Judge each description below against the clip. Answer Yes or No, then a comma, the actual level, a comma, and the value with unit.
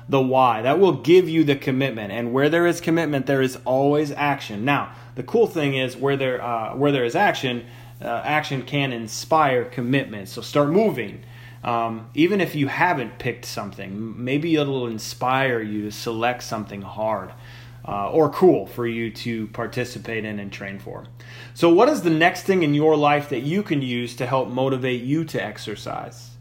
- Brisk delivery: No, average, 185 wpm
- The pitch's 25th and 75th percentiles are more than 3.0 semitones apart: Yes, average, 3.6 semitones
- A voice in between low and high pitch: No, low, 125 Hz